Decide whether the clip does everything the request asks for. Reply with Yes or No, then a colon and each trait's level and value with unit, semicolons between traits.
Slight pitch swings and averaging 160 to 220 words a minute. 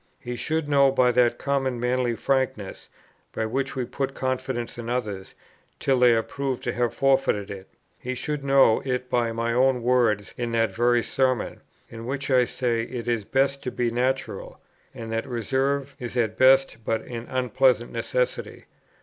Yes: narrow, 2.3 semitones; average, 175 wpm